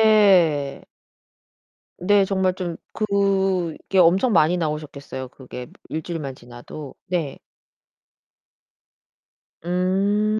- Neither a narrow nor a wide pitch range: Yes, average, 4.6 semitones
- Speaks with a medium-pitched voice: Yes, medium, 180 Hz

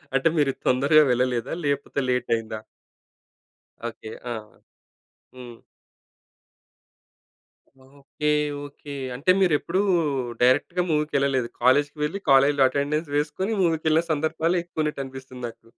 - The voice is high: No, medium, 145 Hz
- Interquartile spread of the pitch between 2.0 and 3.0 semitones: No, average, 3.4 semitones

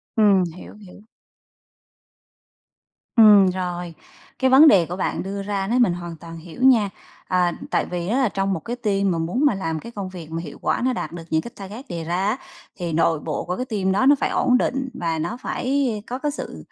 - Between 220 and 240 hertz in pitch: No, high, 195 Hz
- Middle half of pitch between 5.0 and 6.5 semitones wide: Yes, wide, 5.4 semitones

